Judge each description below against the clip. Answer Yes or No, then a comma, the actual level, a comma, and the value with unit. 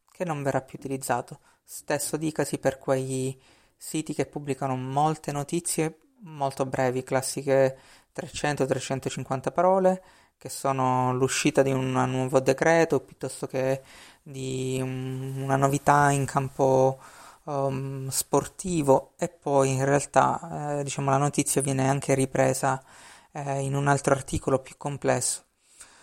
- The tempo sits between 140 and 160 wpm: No, average, 125 wpm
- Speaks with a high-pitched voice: No, low, 135 Hz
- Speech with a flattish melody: Yes, narrow, 1.7 semitones